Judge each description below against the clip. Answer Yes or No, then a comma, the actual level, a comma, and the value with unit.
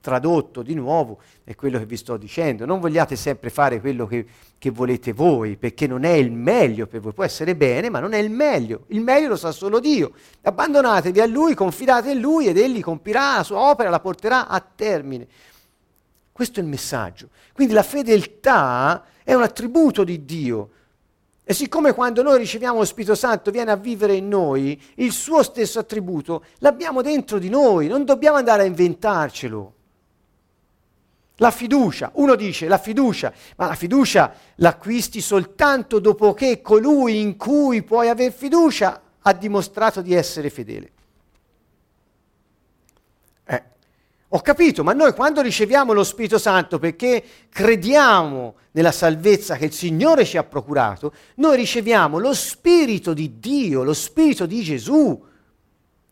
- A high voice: Yes, high, 200 Hz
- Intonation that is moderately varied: No, wide, 8.9 semitones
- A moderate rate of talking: Yes, average, 155 wpm